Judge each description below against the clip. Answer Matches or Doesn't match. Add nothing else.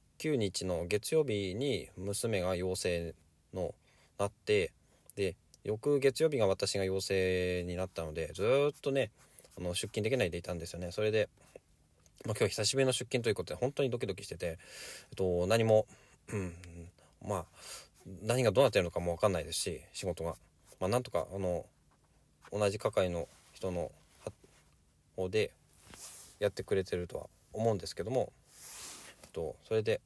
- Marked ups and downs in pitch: Matches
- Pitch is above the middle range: Doesn't match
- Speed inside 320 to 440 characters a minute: Doesn't match